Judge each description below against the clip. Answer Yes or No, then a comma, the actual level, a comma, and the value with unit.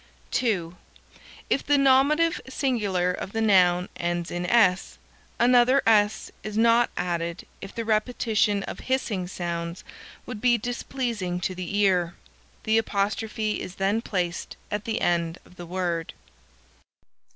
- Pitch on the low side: No, high, 205 Hz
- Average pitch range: Yes, average, 4.7 semitones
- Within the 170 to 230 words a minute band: No, slow, 135 wpm